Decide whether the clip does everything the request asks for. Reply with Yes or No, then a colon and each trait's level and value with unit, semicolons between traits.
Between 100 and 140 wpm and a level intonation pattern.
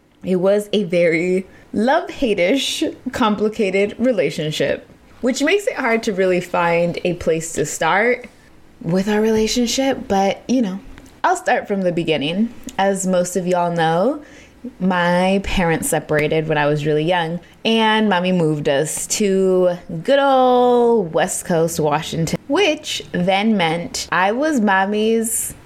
No: slow, 135 wpm; wide, 5.4 semitones